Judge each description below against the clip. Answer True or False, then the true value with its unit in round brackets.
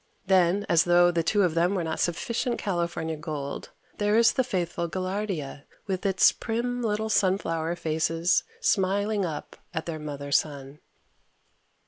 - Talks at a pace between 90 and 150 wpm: True (145 wpm)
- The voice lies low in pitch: False (175 Hz)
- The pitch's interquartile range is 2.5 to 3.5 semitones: False (4.0 semitones)